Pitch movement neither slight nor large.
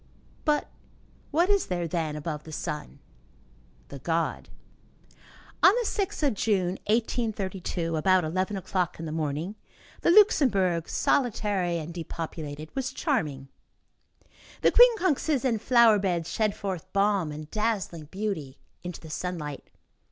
No: wide, 5.8 semitones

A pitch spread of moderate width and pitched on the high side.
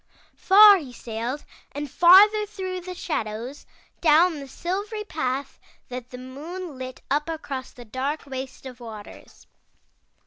No: wide, 6.1 semitones; very high, 290 Hz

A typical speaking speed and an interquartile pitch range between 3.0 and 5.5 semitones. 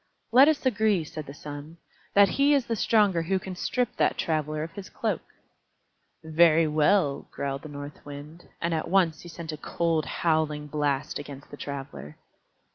Yes: average, 170 wpm; average, 4.5 semitones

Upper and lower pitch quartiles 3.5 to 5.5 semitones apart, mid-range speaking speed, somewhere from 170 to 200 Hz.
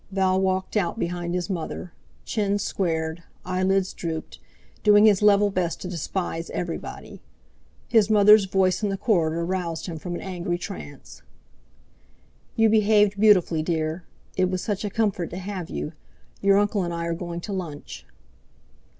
No: average, 3.0 semitones; average, 155 wpm; medium, 185 Hz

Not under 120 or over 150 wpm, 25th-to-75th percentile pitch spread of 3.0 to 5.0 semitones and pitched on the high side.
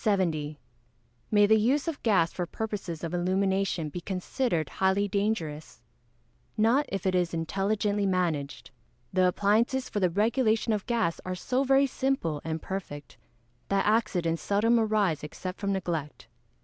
Yes: average, 140 wpm; average, 4.3 semitones; high, 195 Hz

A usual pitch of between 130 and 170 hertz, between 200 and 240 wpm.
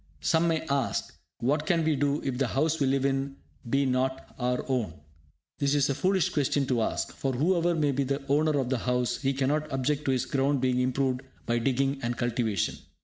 Yes: low, 135 Hz; fast, 205 wpm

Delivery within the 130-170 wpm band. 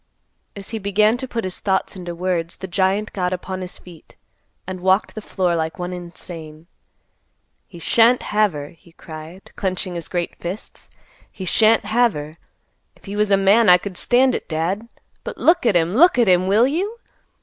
No: average, 190 wpm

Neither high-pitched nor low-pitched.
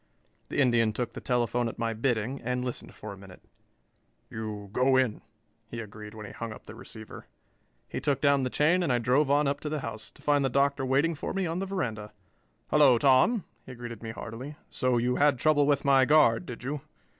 No: low, 125 Hz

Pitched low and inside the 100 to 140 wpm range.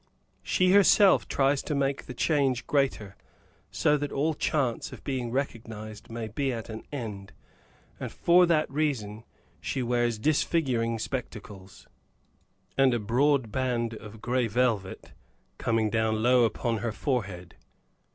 Yes: low, 120 Hz; slow, 135 wpm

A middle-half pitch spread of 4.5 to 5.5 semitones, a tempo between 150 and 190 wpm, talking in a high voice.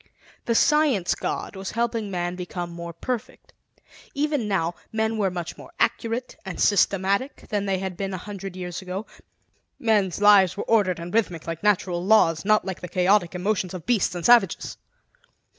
No: average, 3.5 semitones; average, 170 wpm; high, 195 Hz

